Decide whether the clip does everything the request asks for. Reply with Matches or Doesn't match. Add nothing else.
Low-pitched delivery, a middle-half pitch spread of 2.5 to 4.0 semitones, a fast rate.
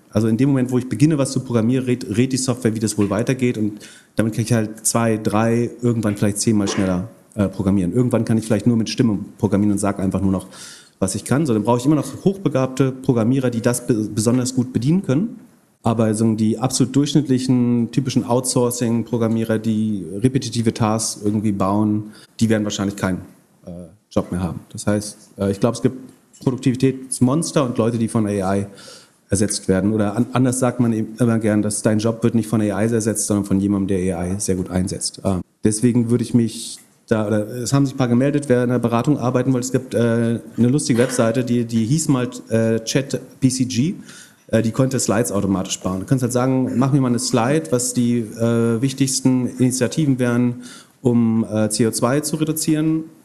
Matches